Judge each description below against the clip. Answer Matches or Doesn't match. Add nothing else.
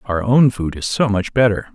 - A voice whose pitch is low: Matches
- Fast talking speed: Matches